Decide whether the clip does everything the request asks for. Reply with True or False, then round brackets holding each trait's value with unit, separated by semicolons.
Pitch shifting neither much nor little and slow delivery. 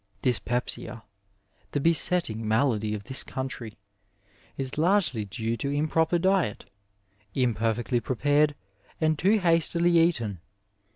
False (6.5 semitones; 110 wpm)